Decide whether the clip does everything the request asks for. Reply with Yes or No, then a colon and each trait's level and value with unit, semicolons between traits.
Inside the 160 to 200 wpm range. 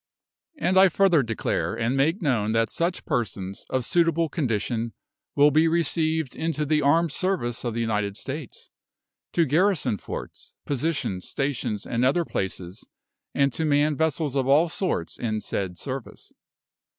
No: average, 150 wpm